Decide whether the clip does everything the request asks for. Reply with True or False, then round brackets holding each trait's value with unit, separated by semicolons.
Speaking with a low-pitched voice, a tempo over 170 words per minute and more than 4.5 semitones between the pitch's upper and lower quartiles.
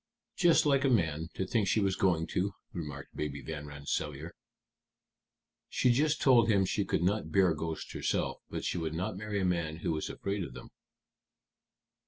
True (90 Hz; 180 wpm; 5.0 semitones)